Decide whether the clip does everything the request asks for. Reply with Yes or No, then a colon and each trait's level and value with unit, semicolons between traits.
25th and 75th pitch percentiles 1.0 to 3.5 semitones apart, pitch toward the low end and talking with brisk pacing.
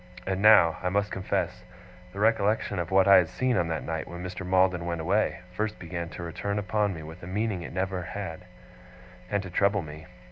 Yes: average, 2.8 semitones; very low, 95 Hz; fast, 215 wpm